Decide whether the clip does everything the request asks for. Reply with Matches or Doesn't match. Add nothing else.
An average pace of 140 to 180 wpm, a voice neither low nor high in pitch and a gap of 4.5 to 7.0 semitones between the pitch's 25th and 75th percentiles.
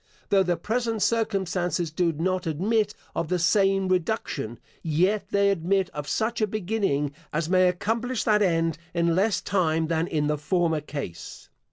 Doesn't match